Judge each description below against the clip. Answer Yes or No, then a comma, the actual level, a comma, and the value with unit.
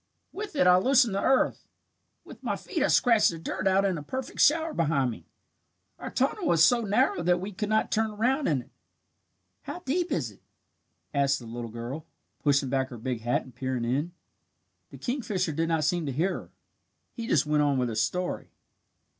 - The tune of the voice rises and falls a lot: Yes, wide, 8.8 semitones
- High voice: No, medium, 170 Hz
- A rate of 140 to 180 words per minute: No, average, 200 wpm